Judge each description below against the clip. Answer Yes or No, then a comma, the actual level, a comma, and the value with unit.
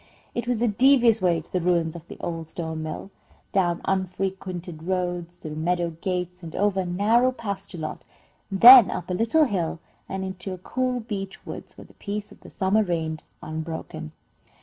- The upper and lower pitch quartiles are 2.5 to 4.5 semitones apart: Yes, average, 3.4 semitones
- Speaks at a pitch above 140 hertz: Yes, medium, 185 Hz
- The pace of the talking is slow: No, average, 180 wpm